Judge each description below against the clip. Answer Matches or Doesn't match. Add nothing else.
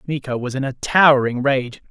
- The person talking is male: Matches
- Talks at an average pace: Matches